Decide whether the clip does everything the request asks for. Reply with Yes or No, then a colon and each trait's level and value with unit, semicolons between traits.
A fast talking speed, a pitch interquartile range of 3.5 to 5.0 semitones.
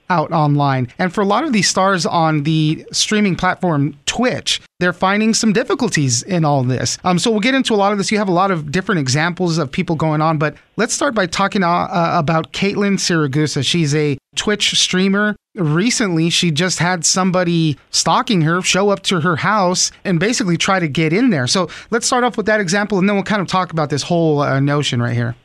Yes: fast, 220 wpm; average, 4.2 semitones